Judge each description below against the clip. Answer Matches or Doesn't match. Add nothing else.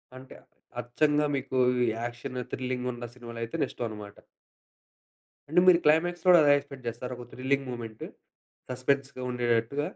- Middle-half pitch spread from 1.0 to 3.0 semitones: Matches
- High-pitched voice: Doesn't match